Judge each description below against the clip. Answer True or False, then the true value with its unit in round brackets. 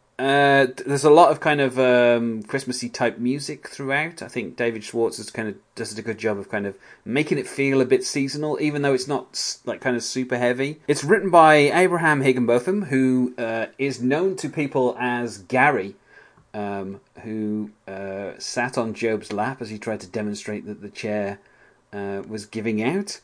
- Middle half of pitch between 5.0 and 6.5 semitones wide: False (4.2 semitones)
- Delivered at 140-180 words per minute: False (190 wpm)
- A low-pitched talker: True (125 Hz)